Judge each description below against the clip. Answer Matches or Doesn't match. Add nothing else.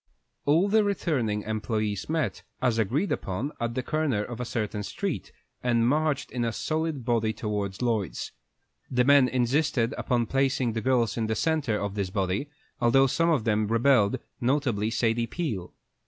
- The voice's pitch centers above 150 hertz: Doesn't match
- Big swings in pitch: Doesn't match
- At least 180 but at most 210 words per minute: Doesn't match